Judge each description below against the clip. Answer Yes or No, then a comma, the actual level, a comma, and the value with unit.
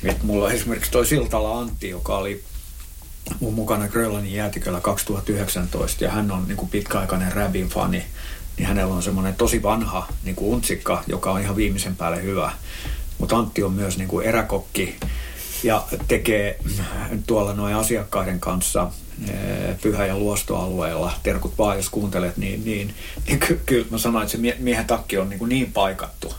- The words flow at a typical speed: No, fast, 160 wpm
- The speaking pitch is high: No, low, 100 Hz